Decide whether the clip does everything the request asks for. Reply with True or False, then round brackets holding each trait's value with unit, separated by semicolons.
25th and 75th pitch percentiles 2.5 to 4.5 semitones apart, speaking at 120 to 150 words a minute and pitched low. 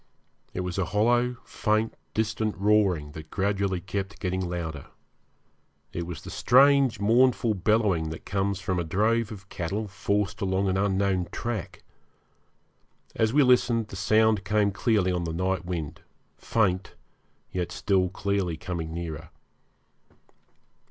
True (3.2 semitones; 135 wpm; 100 Hz)